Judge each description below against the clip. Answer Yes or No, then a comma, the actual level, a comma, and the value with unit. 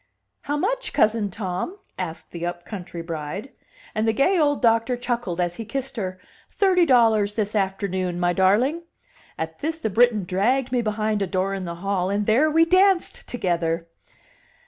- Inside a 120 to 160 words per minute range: No, average, 170 wpm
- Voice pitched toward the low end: No, high, 210 Hz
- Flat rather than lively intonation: No, wide, 5.6 semitones